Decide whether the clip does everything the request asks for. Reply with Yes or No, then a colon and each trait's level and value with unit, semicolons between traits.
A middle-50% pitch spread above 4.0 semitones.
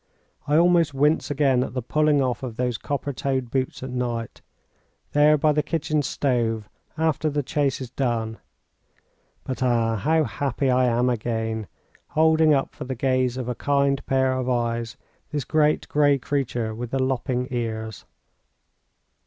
No: average, 3.2 semitones